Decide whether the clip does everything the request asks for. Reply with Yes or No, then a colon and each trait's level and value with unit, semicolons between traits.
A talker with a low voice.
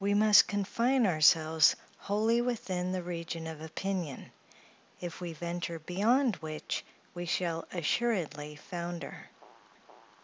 No: medium, 175 Hz